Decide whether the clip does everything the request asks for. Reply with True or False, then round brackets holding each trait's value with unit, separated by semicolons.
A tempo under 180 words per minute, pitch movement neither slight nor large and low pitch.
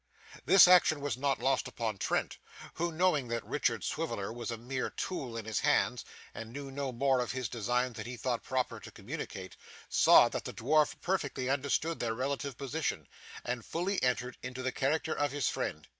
False (190 wpm; 3.3 semitones; 130 Hz)